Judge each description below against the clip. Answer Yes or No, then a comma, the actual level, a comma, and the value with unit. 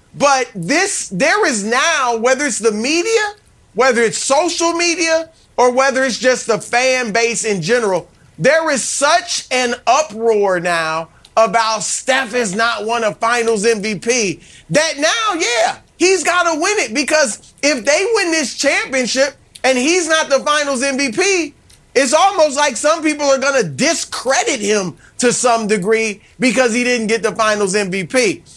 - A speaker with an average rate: Yes, average, 160 wpm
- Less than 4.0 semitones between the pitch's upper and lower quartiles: No, average, 5.3 semitones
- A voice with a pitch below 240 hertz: No, very high, 255 Hz